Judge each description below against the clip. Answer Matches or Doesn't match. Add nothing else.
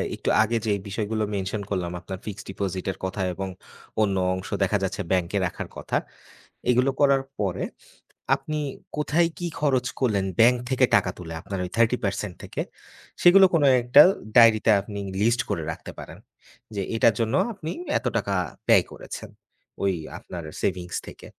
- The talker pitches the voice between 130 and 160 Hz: Doesn't match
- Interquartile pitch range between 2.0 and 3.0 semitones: Doesn't match